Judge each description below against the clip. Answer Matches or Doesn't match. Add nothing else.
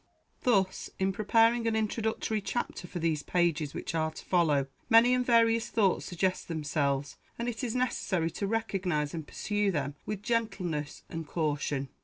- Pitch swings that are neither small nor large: Doesn't match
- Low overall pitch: Doesn't match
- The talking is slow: Doesn't match